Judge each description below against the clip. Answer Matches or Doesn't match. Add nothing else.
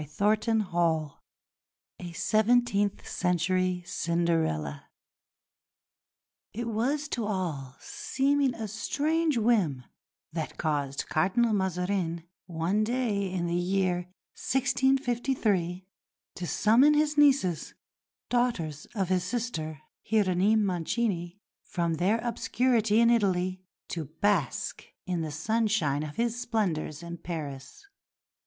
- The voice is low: Doesn't match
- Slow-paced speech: Matches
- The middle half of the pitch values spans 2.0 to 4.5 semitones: Doesn't match